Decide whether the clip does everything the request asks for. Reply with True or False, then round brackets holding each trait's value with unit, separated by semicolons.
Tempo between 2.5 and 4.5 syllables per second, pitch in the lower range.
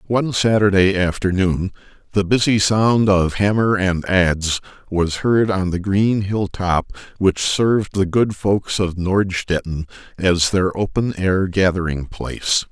True (4.0 syllables/s; 95 Hz)